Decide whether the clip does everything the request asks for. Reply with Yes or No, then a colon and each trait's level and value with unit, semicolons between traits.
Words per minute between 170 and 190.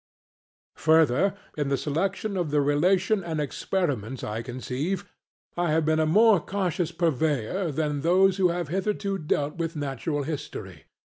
No: average, 145 wpm